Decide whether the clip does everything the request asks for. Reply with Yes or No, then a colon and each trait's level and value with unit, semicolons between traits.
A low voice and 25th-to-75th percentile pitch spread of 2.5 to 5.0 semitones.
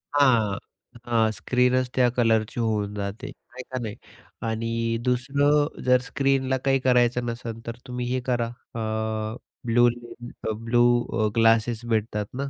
No: low, 120 Hz; narrow, 2.1 semitones